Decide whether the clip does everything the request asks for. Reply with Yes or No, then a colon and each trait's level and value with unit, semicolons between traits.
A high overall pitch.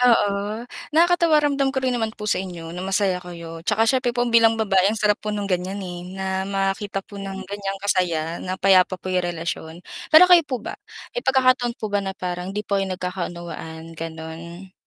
Yes: high, 195 Hz